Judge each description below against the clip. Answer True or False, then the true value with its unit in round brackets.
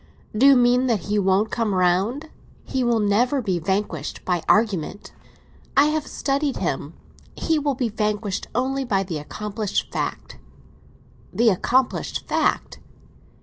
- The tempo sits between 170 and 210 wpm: False (140 wpm)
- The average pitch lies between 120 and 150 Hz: False (220 Hz)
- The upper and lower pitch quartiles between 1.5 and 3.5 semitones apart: False (4.9 semitones)